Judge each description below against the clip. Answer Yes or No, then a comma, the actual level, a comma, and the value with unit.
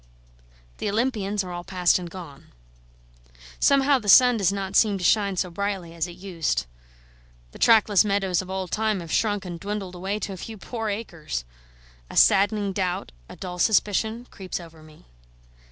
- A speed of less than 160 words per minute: No, average, 170 wpm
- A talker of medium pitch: No, high, 195 Hz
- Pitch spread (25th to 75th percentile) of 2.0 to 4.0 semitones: Yes, average, 2.9 semitones